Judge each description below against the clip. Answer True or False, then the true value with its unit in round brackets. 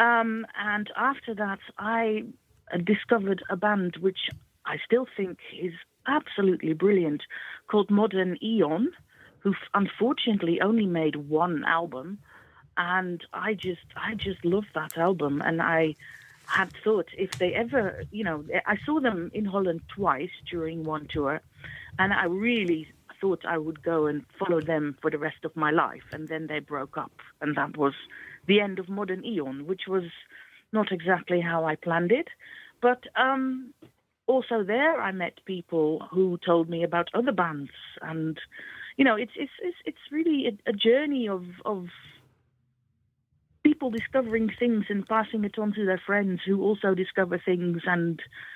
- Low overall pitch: False (185 Hz)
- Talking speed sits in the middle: True (160 wpm)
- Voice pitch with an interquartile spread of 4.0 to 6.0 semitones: True (4.9 semitones)